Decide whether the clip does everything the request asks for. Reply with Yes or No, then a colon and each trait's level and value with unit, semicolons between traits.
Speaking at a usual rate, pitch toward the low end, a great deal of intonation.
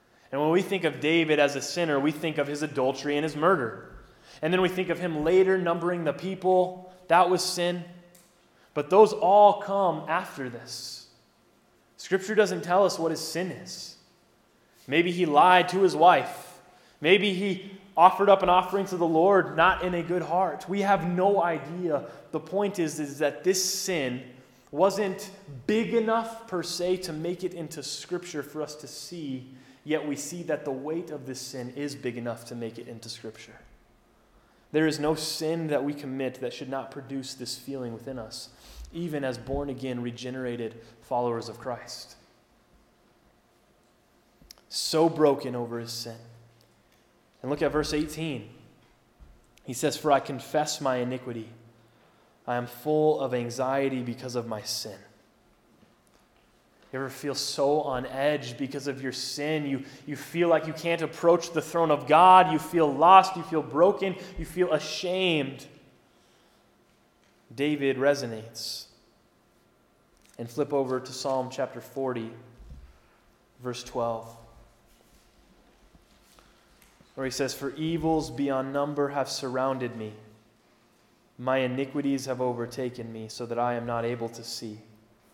No: average, 155 wpm; medium, 145 Hz; wide, 5.7 semitones